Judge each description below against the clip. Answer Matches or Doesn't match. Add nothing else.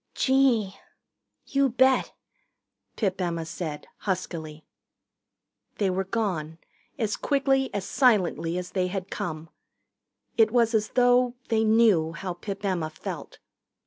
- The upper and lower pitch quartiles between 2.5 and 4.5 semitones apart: Doesn't match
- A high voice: Matches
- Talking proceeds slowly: Matches